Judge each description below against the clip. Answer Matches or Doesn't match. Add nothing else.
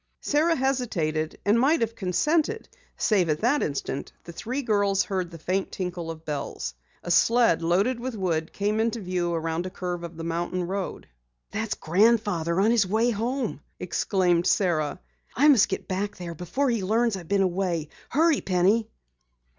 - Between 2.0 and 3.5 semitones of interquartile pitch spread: Doesn't match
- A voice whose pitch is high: Matches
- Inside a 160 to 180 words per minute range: Matches